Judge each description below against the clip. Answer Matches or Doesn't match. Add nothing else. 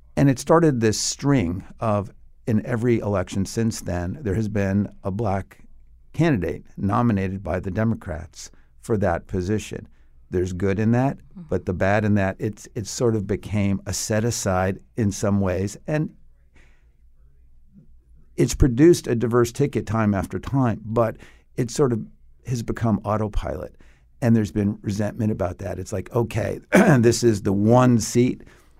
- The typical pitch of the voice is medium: Doesn't match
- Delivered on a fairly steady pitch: Doesn't match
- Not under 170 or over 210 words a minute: Doesn't match